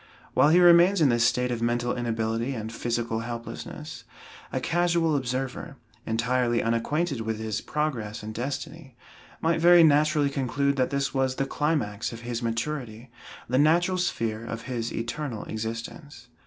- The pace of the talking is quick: No, average, 150 wpm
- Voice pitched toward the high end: No, low, 125 Hz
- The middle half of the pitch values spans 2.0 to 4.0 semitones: No, average, 4.6 semitones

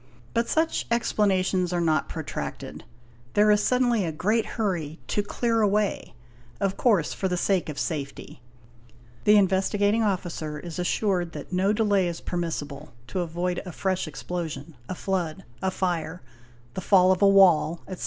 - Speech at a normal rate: Yes, average, 155 wpm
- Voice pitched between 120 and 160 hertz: No, medium, 185 Hz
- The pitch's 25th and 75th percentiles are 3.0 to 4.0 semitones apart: Yes, average, 3.4 semitones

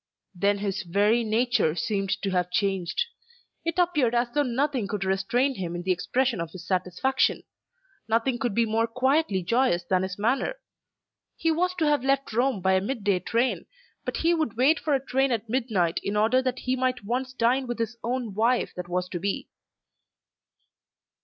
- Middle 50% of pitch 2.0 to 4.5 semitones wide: No, average, 5.1 semitones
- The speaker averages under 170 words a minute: No, average, 185 wpm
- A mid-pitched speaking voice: No, high, 230 Hz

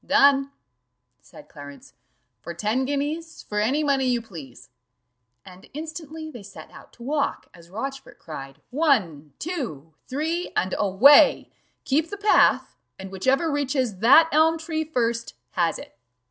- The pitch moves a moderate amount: No, wide, 8.2 semitones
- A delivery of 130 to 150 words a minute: Yes, average, 140 wpm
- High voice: Yes, very high, 260 Hz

